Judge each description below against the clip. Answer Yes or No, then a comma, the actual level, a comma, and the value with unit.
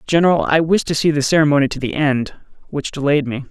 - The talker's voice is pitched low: No, medium, 145 Hz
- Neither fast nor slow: No, fast, 220 wpm